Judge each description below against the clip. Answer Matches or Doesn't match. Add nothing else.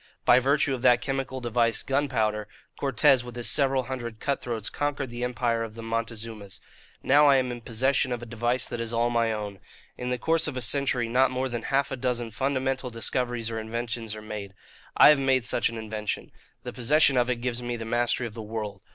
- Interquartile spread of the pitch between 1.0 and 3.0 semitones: Matches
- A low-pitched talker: Matches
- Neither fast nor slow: Doesn't match